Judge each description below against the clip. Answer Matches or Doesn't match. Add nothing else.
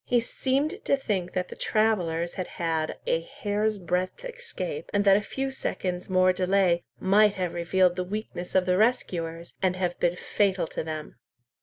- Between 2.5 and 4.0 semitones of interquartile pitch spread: Matches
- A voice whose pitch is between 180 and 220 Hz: Matches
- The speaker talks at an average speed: Matches